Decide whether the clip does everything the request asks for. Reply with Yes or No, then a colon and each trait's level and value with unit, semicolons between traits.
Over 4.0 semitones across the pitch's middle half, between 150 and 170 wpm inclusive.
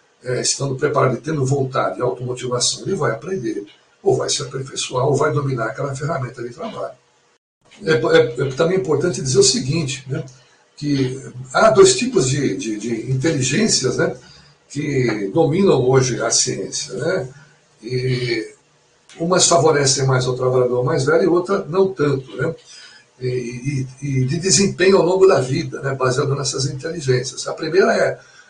Yes: average, 4.4 semitones; average, 155 wpm